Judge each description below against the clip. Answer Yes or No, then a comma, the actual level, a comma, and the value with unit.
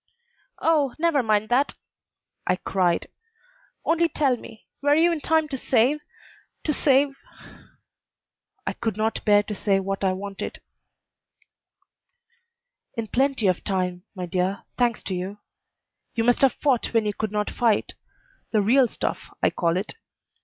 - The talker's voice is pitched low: No, high, 225 Hz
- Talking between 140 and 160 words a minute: Yes, average, 150 wpm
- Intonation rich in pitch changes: Yes, wide, 5.8 semitones